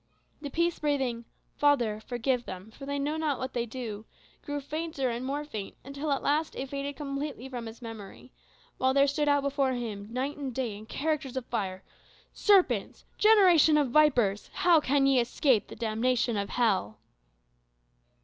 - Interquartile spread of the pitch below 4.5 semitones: Yes, average, 3.8 semitones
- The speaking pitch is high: Yes, very high, 265 Hz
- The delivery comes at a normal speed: Yes, average, 170 wpm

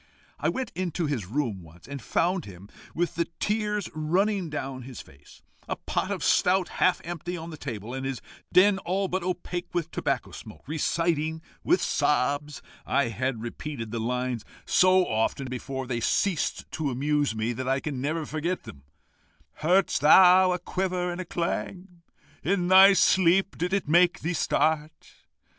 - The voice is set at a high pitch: No, medium, 155 Hz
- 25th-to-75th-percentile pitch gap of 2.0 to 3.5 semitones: No, wide, 5.4 semitones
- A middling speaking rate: Yes, average, 165 wpm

